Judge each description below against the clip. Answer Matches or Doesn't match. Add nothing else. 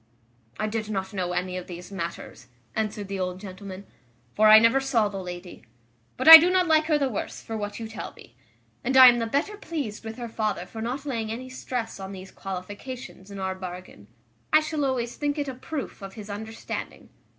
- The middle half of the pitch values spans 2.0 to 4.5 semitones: Doesn't match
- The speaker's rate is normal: Doesn't match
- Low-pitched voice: Doesn't match